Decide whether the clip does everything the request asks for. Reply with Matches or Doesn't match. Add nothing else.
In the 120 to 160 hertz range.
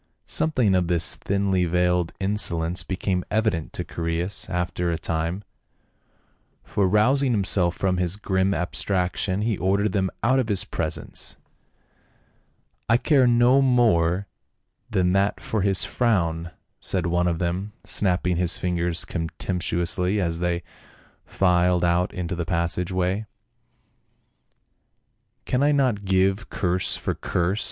Doesn't match